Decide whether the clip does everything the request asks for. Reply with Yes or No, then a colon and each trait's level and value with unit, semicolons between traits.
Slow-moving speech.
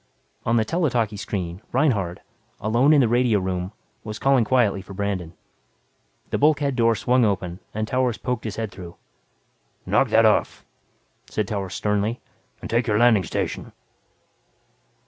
No: average, 150 wpm